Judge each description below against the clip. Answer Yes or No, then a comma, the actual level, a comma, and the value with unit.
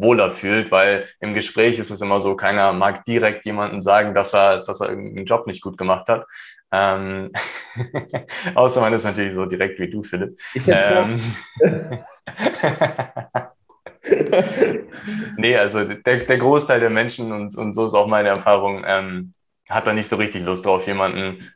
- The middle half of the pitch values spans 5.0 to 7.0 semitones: No, average, 2.8 semitones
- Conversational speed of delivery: Yes, average, 160 wpm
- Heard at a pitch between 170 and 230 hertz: No, low, 105 Hz